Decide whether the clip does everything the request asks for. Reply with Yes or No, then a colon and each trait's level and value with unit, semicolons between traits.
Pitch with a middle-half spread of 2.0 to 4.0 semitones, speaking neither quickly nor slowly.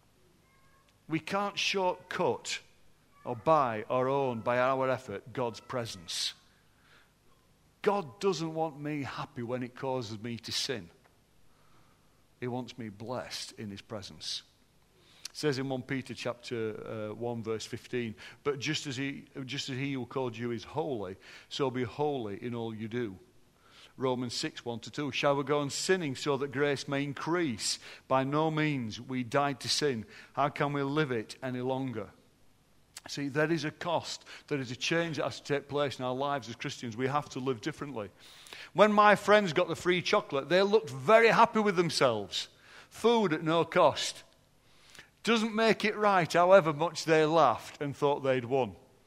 No: average, 4.5 semitones; average, 170 wpm